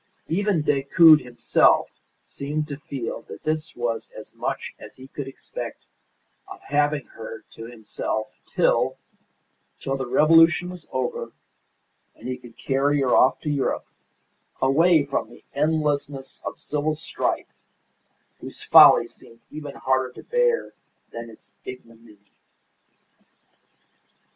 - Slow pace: Yes, slow, 125 wpm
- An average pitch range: Yes, average, 3.5 semitones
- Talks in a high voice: No, medium, 140 Hz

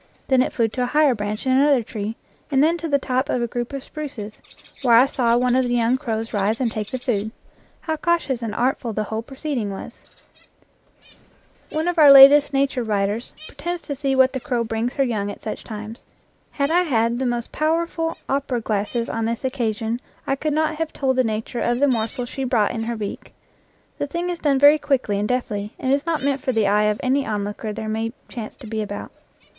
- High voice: Yes, high, 245 Hz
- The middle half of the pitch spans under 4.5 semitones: Yes, average, 4.0 semitones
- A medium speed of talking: No, fast, 225 wpm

